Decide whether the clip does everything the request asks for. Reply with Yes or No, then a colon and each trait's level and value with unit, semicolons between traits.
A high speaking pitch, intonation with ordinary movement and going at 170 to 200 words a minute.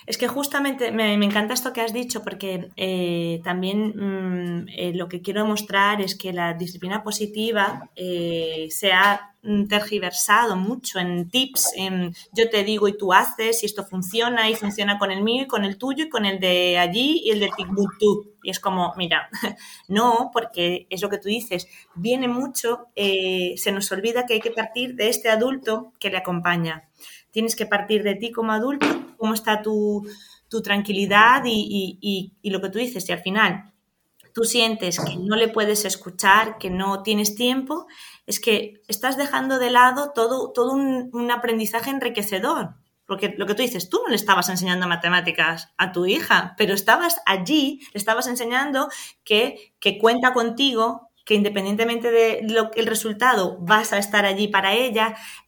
Yes: high, 210 Hz; average, 3.3 semitones; average, 180 wpm